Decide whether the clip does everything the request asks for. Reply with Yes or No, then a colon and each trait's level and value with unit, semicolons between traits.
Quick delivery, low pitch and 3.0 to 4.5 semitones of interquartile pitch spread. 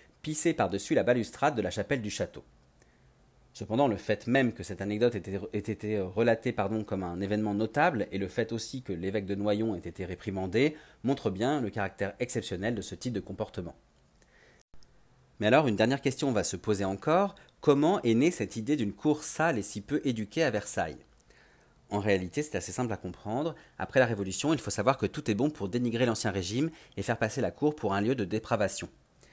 No: average, 205 wpm; low, 110 Hz; average, 4.2 semitones